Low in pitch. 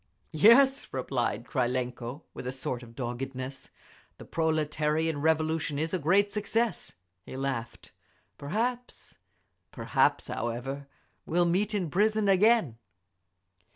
No: medium, 155 Hz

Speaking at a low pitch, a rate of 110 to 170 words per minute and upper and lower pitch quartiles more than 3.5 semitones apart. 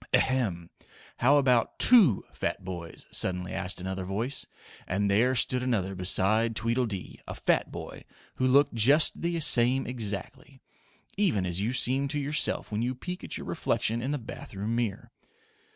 Yes: low, 115 Hz; average, 160 wpm; average, 5.2 semitones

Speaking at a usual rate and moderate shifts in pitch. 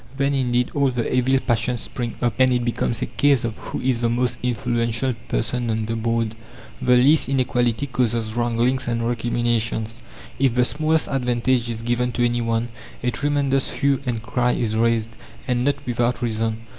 No: average, 180 wpm; narrow, 1.7 semitones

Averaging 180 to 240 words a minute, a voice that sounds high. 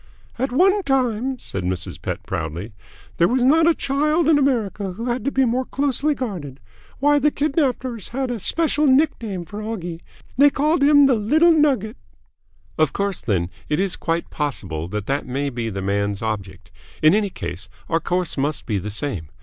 Yes: average, 185 wpm; high, 210 Hz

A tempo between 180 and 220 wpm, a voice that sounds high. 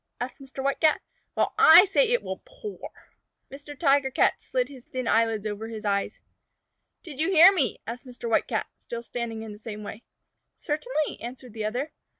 Yes: average, 185 wpm; very high, 255 Hz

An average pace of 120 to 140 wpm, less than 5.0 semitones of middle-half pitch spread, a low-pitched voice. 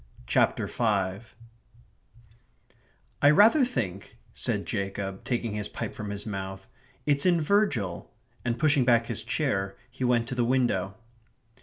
No: slow, 135 wpm; average, 5.3 semitones; low, 115 Hz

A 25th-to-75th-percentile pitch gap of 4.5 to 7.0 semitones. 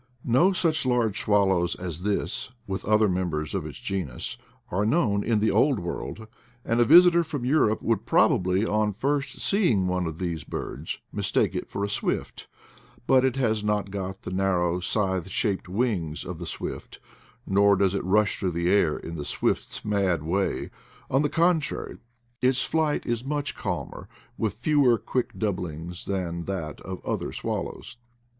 Yes: average, 5.2 semitones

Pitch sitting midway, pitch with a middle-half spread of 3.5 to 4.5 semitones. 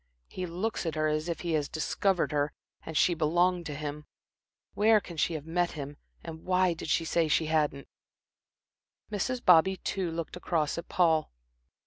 No: medium, 165 Hz; average, 2.7 semitones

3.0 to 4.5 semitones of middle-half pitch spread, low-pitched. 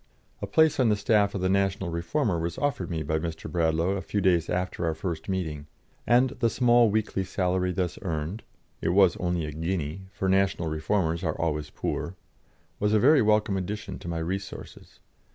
Yes: average, 3.8 semitones; very low, 95 Hz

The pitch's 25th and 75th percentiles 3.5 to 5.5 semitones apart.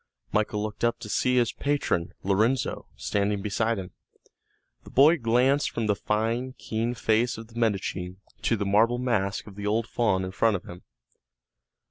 No: average, 2.8 semitones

